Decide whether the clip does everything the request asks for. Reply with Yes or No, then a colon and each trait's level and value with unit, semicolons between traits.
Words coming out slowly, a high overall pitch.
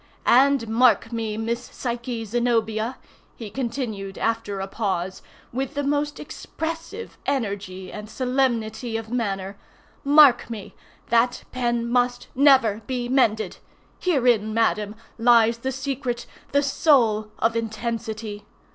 Yes: slow, 110 wpm; high, 235 Hz